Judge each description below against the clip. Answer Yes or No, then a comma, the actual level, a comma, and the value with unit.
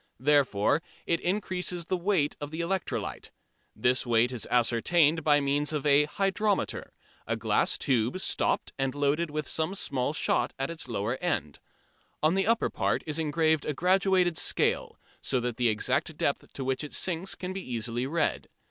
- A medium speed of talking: Yes, average, 170 wpm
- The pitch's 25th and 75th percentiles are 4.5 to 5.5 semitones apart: Yes, average, 5.1 semitones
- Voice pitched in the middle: Yes, medium, 150 Hz